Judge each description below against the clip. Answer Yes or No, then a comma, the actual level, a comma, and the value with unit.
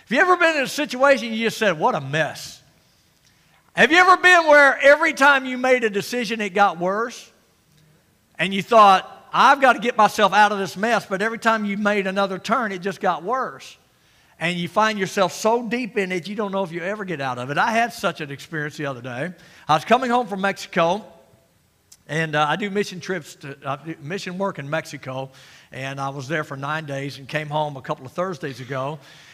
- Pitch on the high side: Yes, high, 195 Hz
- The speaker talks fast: Yes, fast, 225 wpm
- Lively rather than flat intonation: Yes, wide, 6.8 semitones